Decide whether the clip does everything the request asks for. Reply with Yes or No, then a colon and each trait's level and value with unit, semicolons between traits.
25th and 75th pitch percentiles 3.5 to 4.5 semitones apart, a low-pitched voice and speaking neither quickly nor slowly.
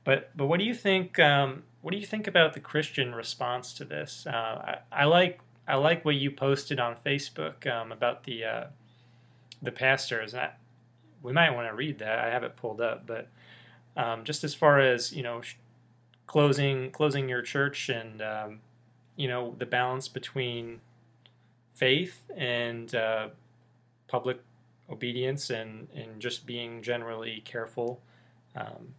No: average, 2.8 semitones; low, 125 Hz; average, 160 wpm